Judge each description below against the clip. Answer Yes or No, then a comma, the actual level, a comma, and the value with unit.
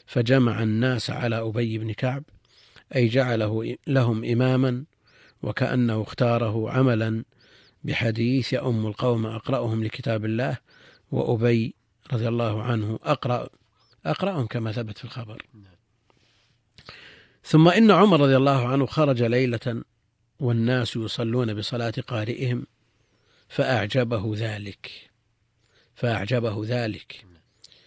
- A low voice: Yes, low, 120 Hz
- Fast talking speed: No, average, 95 wpm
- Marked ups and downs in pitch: No, narrow, 2.4 semitones